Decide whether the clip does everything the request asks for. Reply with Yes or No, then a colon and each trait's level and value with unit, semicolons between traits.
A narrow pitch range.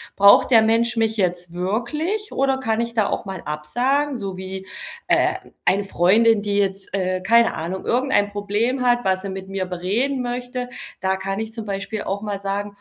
No: average, 3.8 semitones